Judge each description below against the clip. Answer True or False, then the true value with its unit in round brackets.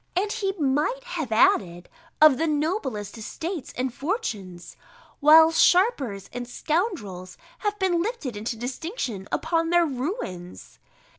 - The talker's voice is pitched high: True (300 Hz)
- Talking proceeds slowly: True (125 wpm)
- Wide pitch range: True (8.3 semitones)